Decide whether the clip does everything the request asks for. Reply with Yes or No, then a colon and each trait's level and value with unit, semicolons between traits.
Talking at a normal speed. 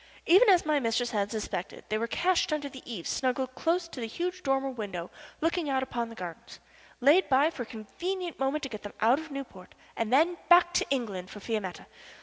No: fast, 210 wpm